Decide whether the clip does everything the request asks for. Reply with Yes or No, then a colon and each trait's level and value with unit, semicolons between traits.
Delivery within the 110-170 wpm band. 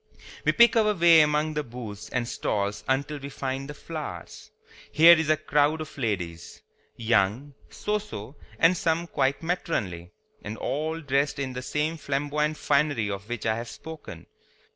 Yes: average, 165 wpm